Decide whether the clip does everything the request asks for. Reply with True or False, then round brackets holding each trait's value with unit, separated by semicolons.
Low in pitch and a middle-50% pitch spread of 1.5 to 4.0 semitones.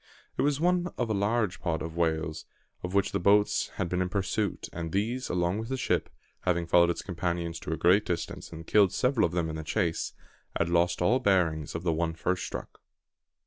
True (90 Hz; 3.7 semitones)